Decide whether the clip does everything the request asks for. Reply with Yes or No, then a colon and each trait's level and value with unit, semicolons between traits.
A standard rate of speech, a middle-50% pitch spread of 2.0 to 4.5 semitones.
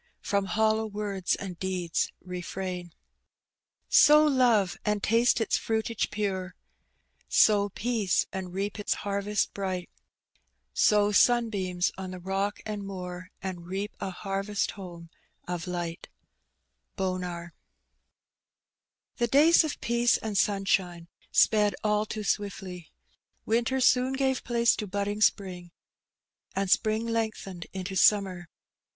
No: slow, 120 wpm; average, 2.9 semitones